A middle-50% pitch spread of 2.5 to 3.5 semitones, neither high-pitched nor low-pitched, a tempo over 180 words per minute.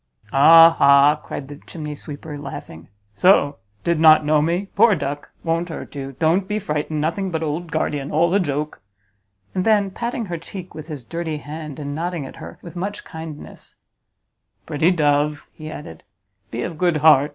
No: average, 2.8 semitones; medium, 155 Hz; average, 175 wpm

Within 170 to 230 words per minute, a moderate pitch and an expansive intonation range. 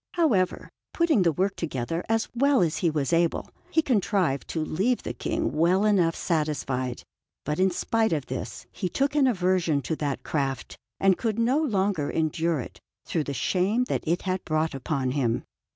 Yes: average, 180 wpm; medium, 175 Hz; wide, 5.9 semitones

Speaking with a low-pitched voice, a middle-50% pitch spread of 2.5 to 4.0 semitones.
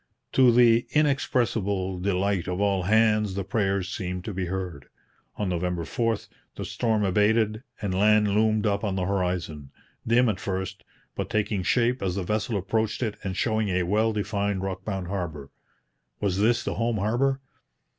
Yes: low, 100 Hz; average, 3.0 semitones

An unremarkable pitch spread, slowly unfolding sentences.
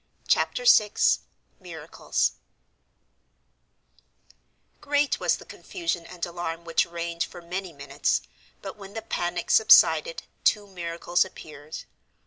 Yes: average, 3.7 semitones; slow, 110 wpm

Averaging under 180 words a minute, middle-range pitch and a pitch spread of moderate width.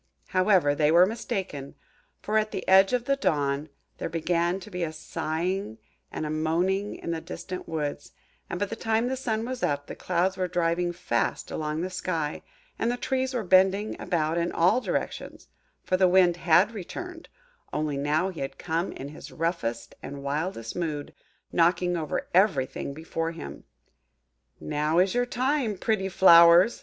Yes: average, 165 wpm; medium, 175 Hz; average, 4.0 semitones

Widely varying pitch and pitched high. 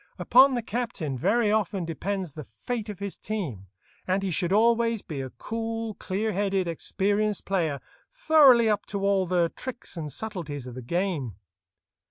No: average, 4.9 semitones; high, 195 Hz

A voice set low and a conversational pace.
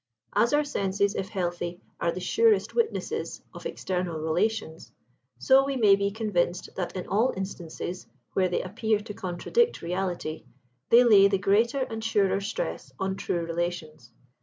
No: high, 195 Hz; average, 155 wpm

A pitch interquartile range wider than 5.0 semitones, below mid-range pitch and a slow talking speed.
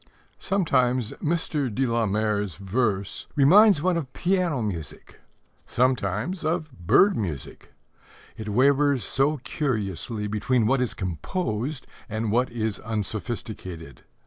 Yes: wide, 5.6 semitones; low, 120 Hz; slow, 115 wpm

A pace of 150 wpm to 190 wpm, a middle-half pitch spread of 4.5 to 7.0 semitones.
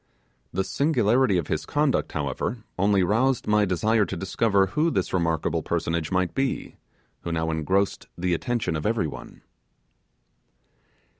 No: average, 140 wpm; average, 5.1 semitones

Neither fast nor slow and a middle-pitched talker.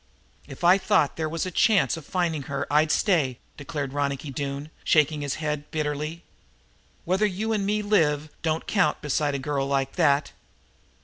Yes: average, 165 wpm; medium, 155 Hz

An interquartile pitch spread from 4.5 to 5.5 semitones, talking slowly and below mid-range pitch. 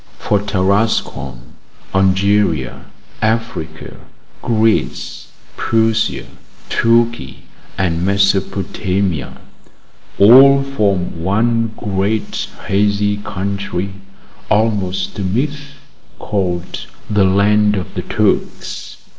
No: average, 2.8 semitones; slow, 75 wpm; low, 100 Hz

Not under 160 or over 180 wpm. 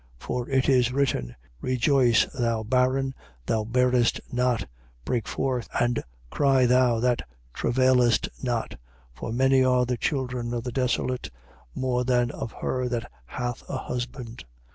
No: average, 140 wpm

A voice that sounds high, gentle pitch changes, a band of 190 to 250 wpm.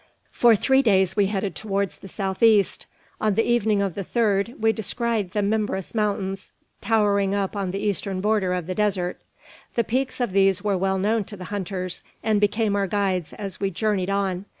Yes: high, 200 Hz; narrow, 2.0 semitones; average, 195 wpm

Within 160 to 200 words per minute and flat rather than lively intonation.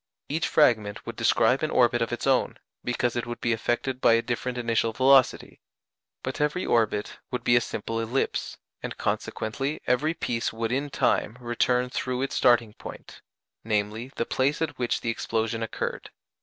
Yes: average, 170 wpm; narrow, 2.3 semitones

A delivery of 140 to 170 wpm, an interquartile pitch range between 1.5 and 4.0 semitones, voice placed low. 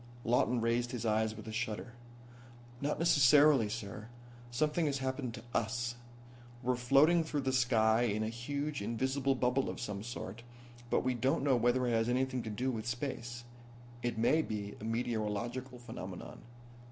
Yes: average, 165 wpm; average, 2.8 semitones; low, 120 Hz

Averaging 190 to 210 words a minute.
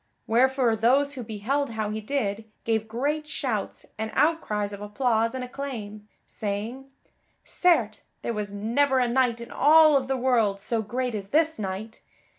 No: average, 155 wpm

